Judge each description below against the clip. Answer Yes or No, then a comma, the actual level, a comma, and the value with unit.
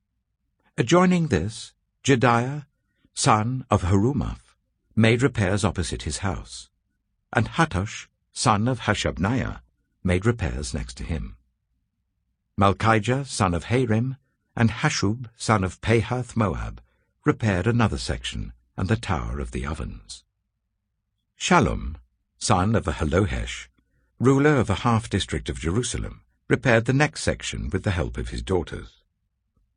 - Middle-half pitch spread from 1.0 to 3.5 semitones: No, average, 4.6 semitones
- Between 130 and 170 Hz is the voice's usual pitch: No, low, 105 Hz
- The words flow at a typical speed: No, slow, 120 wpm